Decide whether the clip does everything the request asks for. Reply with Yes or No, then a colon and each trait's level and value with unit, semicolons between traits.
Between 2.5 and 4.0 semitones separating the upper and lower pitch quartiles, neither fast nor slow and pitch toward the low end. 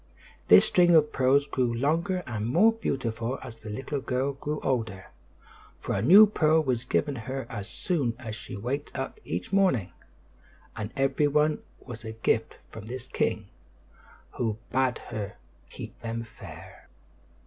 No: average, 4.6 semitones; average, 155 wpm; low, 130 Hz